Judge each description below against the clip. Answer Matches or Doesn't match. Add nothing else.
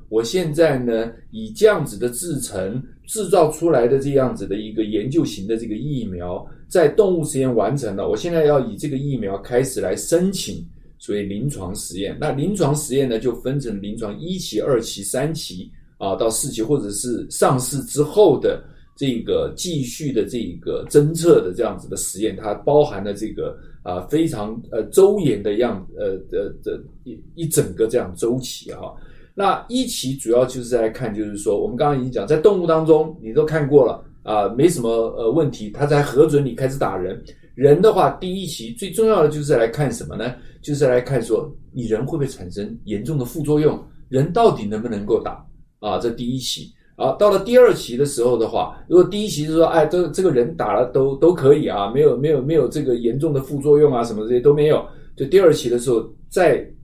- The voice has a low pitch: Doesn't match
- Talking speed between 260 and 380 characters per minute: Matches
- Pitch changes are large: Matches